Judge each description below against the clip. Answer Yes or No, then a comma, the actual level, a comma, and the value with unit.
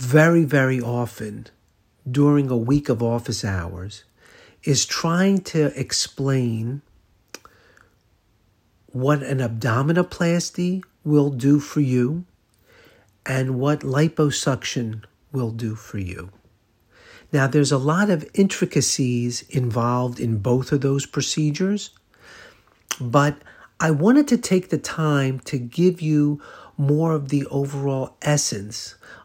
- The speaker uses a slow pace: Yes, slow, 110 wpm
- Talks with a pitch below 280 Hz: Yes, low, 135 Hz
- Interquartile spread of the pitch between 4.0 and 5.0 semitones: Yes, average, 4.5 semitones